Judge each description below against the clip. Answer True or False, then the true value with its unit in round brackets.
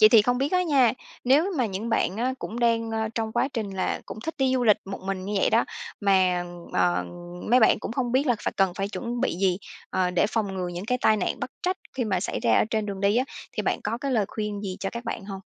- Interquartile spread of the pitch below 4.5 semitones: True (4.1 semitones)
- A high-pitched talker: True (220 Hz)